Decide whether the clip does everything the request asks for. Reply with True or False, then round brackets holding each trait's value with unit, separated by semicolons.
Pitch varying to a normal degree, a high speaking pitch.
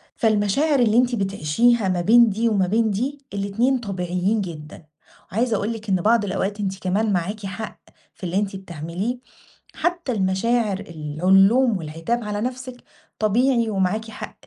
True (3.7 semitones; 210 Hz)